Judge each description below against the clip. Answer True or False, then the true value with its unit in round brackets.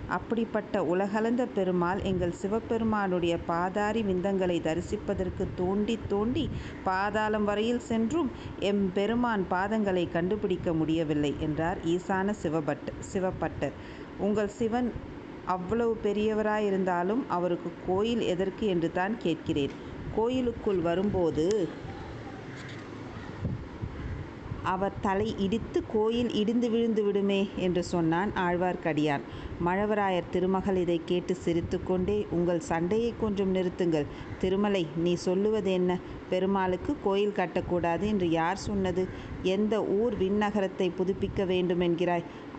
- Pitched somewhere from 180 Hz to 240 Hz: True (190 Hz)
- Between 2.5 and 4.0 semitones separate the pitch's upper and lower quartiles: True (3.1 semitones)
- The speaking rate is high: False (95 wpm)